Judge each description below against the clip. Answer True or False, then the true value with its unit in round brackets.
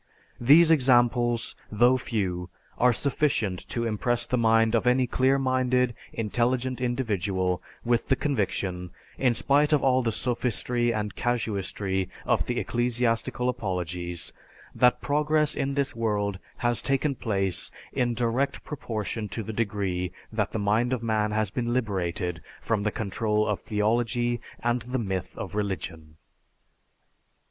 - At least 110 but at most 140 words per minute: True (135 wpm)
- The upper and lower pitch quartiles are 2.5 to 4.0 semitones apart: True (3.4 semitones)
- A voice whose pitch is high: False (115 Hz)